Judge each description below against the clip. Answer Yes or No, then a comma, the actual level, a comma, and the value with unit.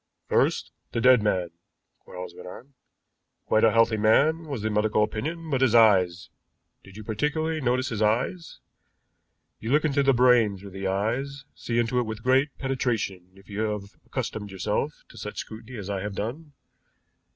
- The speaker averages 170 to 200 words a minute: Yes, average, 175 wpm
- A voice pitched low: Yes, low, 115 Hz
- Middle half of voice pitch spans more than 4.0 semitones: Yes, average, 4.4 semitones